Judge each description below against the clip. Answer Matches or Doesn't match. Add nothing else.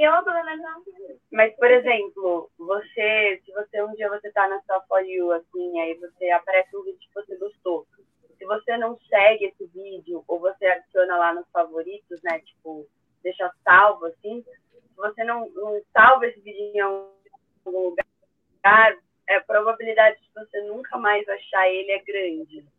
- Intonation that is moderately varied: Matches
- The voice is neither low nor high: Doesn't match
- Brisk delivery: Doesn't match